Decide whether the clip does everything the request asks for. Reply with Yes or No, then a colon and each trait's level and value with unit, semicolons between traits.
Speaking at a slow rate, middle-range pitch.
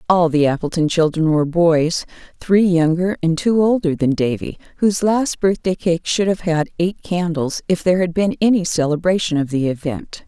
No: average, 175 wpm; medium, 170 Hz